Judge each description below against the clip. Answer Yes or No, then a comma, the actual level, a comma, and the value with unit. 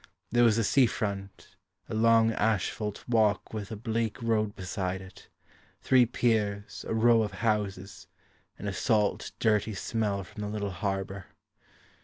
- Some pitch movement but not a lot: No, narrow, 2.1 semitones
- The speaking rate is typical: Yes, average, 150 wpm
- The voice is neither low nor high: No, low, 105 Hz